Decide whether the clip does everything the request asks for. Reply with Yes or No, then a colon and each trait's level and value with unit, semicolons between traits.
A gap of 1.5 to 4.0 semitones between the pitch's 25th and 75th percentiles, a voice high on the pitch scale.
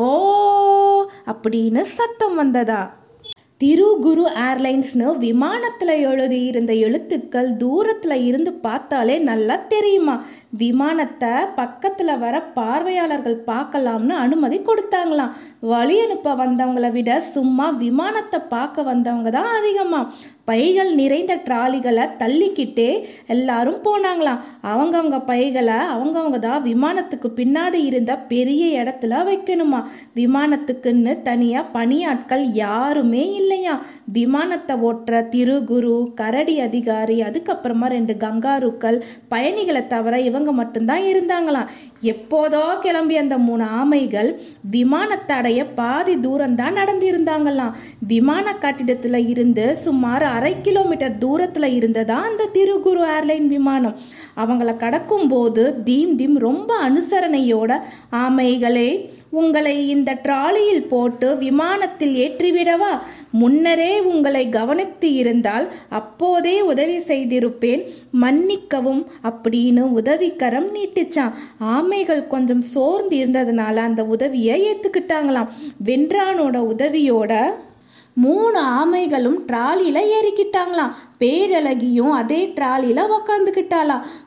No: wide, 5.4 semitones; very high, 275 Hz